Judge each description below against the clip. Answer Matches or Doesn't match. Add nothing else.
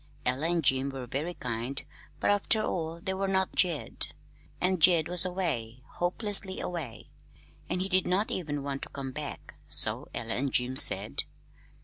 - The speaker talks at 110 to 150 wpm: Doesn't match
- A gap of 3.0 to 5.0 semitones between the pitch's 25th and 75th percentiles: Doesn't match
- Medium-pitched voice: Matches